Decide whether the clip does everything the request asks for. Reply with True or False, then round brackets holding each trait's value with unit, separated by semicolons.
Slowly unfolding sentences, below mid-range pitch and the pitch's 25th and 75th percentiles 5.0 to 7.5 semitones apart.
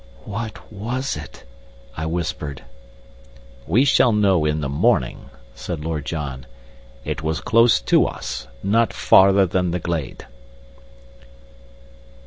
True (115 wpm; 85 Hz; 5.5 semitones)